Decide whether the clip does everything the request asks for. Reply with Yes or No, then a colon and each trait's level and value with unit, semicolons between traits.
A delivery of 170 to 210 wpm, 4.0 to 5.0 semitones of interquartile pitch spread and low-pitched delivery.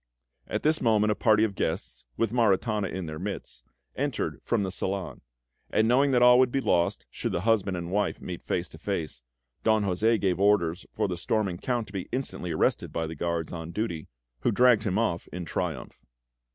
Yes: average, 200 wpm; average, 4.5 semitones; low, 100 Hz